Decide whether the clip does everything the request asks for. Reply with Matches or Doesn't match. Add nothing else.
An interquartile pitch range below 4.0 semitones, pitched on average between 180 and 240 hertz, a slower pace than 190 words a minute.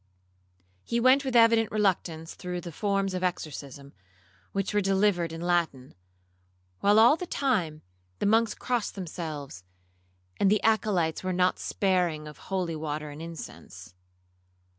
Doesn't match